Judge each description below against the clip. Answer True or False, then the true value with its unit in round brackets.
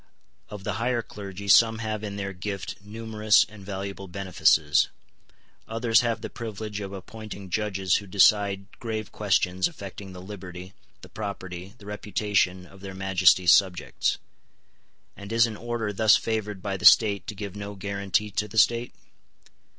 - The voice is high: False (100 Hz)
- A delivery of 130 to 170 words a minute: True (155 wpm)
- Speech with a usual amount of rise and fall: False (2.0 semitones)